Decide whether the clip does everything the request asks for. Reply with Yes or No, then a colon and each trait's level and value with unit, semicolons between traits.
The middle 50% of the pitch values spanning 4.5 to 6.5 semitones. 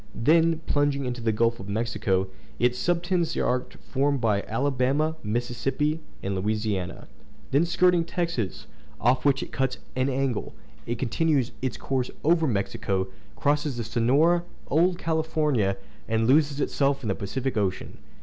Yes: average, 5.2 semitones